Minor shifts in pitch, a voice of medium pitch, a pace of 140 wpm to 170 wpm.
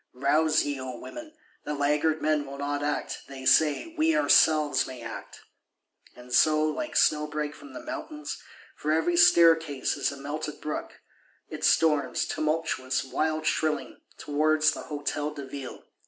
Yes: narrow, 2.0 semitones; medium, 150 Hz; average, 150 wpm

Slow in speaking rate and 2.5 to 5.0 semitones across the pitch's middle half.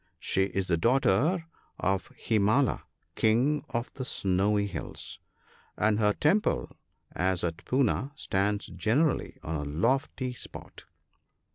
No: slow, 120 wpm; wide, 5.5 semitones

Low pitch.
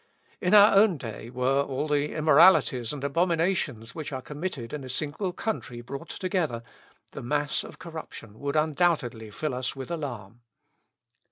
No: medium, 145 Hz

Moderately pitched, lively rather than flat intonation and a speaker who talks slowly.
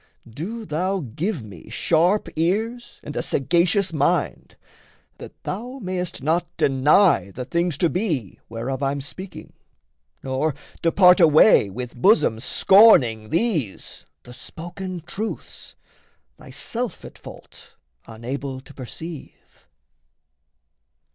Yes: medium, 160 Hz; wide, 6.2 semitones; slow, 110 wpm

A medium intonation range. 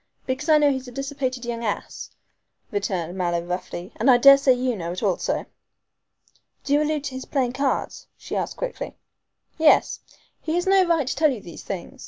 No: wide, 6.1 semitones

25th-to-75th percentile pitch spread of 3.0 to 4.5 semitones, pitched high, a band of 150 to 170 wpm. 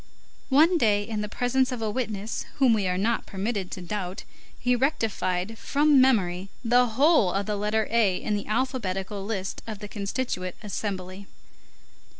Yes: average, 4.1 semitones; high, 210 Hz; average, 160 wpm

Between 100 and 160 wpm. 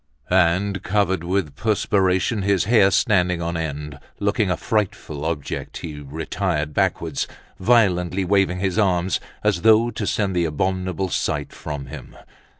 Yes: average, 145 wpm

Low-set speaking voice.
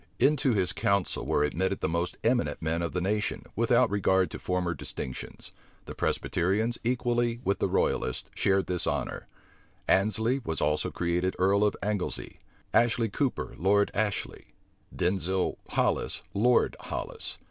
Yes: low, 100 Hz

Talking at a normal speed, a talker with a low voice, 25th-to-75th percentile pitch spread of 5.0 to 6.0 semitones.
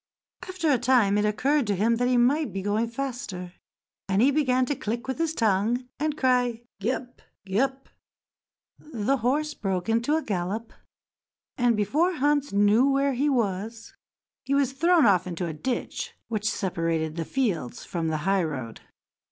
No: average, 170 wpm; high, 235 Hz; wide, 5.6 semitones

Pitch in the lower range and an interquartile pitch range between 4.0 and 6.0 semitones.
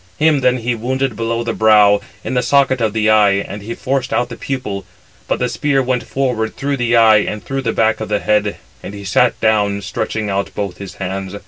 No: low, 110 Hz; average, 3.6 semitones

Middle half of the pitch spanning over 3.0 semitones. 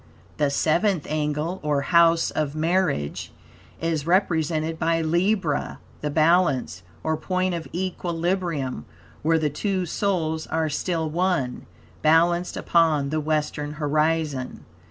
No: narrow, 2.5 semitones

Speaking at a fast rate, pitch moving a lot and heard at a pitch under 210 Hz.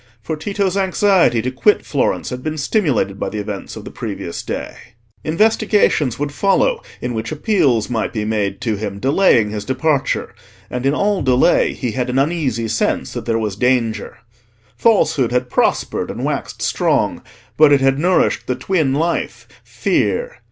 No: average, 165 wpm; wide, 7.1 semitones; low, 135 Hz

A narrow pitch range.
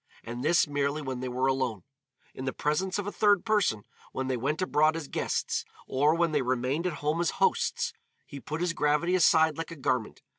No: average, 4.2 semitones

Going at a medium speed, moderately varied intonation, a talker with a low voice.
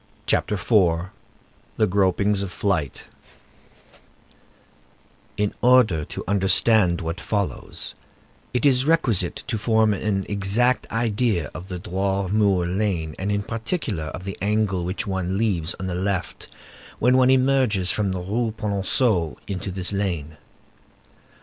No: slow, 130 wpm; average, 3.2 semitones; low, 100 Hz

